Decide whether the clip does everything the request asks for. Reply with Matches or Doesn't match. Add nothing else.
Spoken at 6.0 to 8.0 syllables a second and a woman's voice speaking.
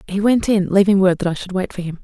Matches